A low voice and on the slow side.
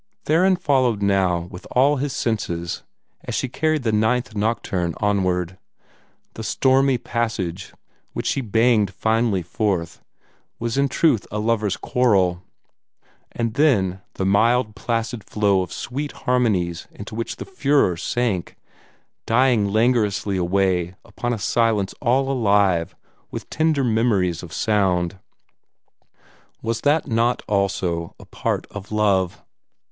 Yes: low, 110 Hz; slow, 125 wpm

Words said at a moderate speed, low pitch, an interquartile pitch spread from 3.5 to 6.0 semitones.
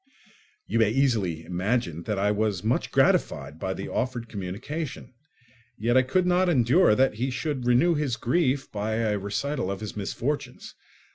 Yes: average, 160 wpm; low, 115 Hz; average, 4.8 semitones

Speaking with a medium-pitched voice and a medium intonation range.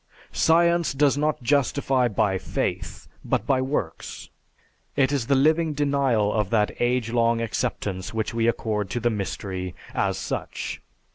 No: low, 120 Hz; average, 4.7 semitones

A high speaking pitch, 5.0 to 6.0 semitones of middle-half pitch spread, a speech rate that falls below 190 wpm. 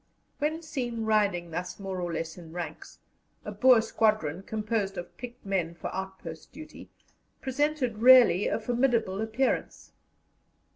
Yes: high, 215 Hz; wide, 5.4 semitones; slow, 135 wpm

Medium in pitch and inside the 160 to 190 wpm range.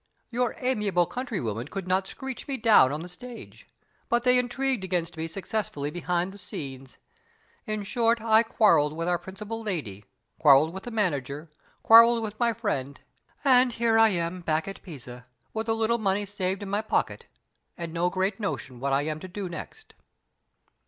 No: high, 195 Hz; average, 175 wpm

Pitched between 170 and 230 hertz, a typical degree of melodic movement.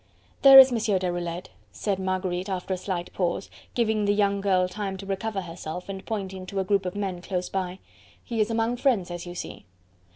No: high, 190 Hz; narrow, 2.3 semitones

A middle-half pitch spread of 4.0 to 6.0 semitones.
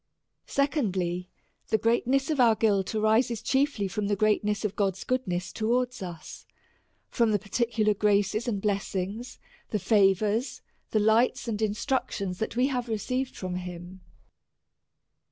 No: average, 3.4 semitones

